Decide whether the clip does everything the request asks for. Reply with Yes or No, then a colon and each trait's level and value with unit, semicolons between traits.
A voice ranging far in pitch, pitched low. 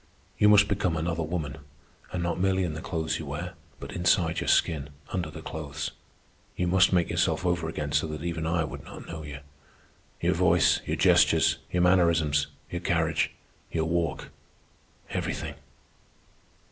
No: narrow, 2.4 semitones; very low, 80 Hz